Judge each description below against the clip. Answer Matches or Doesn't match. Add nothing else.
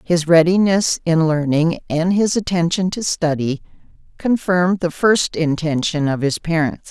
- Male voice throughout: Doesn't match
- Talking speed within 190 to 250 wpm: Doesn't match